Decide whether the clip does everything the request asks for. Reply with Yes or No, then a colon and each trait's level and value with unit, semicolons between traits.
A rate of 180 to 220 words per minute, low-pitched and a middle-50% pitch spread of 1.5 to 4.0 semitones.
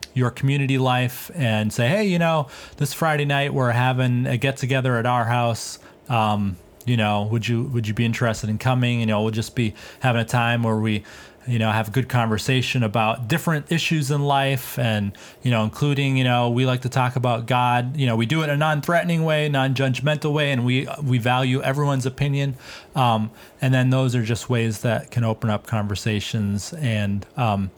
Yes: fast, 205 wpm; low, 125 Hz; average, 3.2 semitones